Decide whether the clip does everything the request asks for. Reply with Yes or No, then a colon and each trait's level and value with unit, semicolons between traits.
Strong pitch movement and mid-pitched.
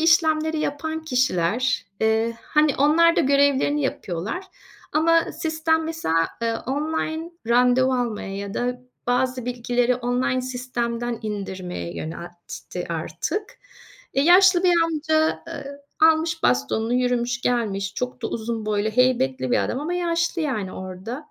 No: wide, 6.2 semitones; very high, 250 Hz